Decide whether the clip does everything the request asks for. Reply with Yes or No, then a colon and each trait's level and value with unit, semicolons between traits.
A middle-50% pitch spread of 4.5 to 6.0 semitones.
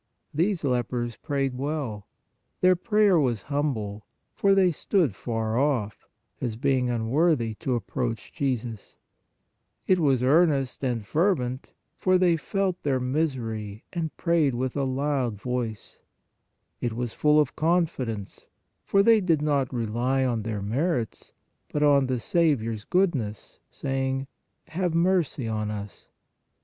Yes: wide, 5.6 semitones